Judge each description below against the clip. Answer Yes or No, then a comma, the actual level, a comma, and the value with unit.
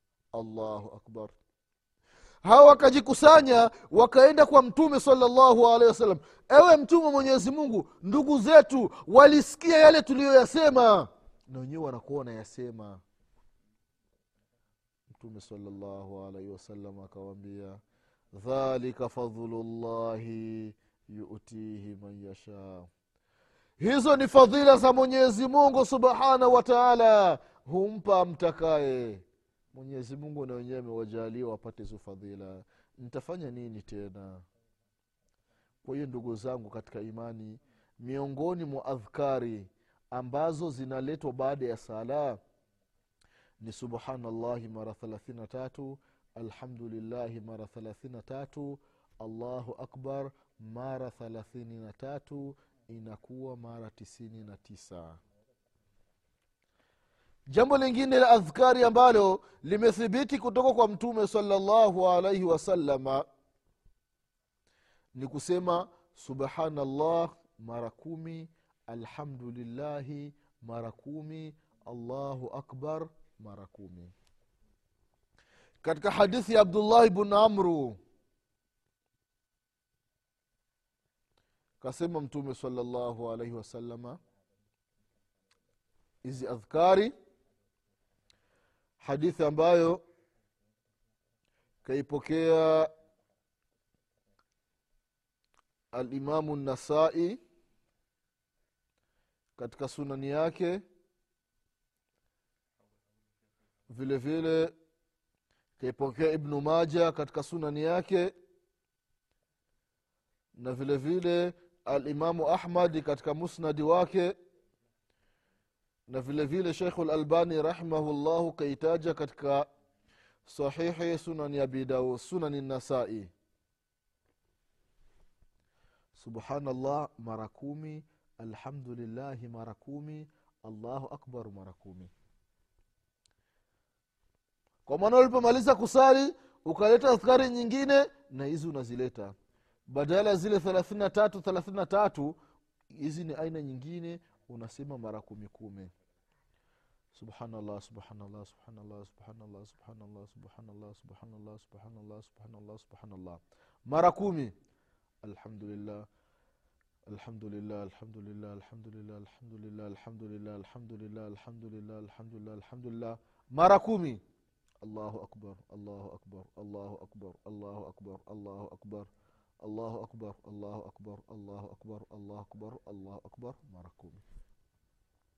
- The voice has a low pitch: Yes, low, 125 Hz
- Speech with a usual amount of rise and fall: No, wide, 7.5 semitones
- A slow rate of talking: Yes, slow, 90 wpm